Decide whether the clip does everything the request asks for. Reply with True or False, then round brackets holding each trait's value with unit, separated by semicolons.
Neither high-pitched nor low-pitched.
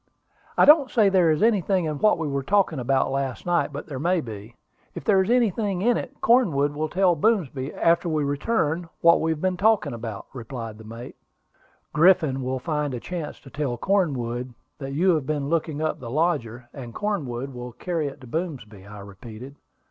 True (150 Hz)